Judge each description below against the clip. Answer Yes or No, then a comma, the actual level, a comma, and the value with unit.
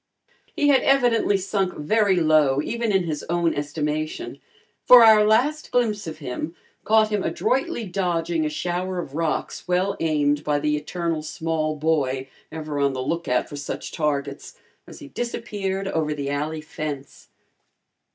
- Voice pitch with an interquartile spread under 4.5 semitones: No, average, 5.3 semitones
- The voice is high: No, medium, 165 Hz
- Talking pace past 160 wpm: No, average, 150 wpm